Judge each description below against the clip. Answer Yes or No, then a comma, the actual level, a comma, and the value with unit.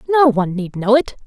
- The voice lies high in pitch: Yes, high, 235 Hz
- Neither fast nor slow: No, fast, 235 wpm